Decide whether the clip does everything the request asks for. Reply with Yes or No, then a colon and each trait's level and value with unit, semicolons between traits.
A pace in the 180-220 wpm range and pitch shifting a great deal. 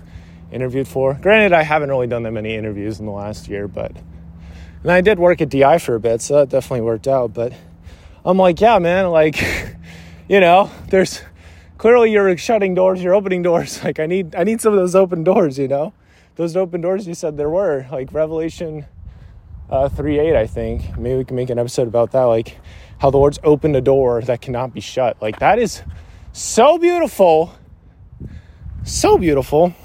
Yes: average, 195 wpm; wide, 8.7 semitones